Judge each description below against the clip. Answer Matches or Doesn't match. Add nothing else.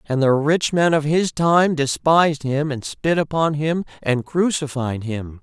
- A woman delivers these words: Doesn't match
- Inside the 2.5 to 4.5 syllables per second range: Matches